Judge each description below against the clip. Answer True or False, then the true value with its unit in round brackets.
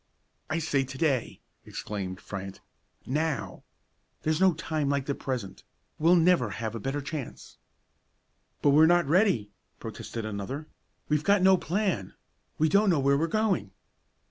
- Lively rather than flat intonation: True (5.8 semitones)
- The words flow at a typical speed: True (145 wpm)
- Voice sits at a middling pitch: True (145 Hz)